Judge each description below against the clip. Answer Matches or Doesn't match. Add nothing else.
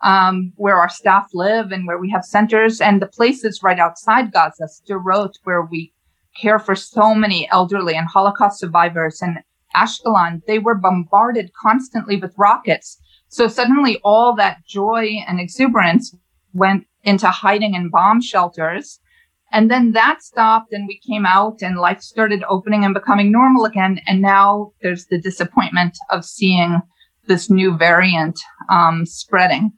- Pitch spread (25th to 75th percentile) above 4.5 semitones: Doesn't match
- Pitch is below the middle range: Doesn't match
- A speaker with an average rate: Matches